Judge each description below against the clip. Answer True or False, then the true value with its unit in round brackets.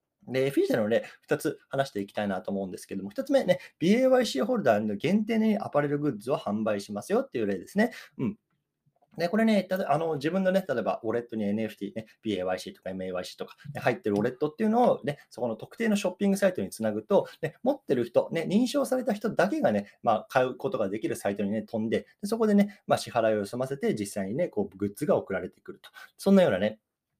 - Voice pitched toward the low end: False (145 Hz)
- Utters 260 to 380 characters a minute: False (470 characters per minute)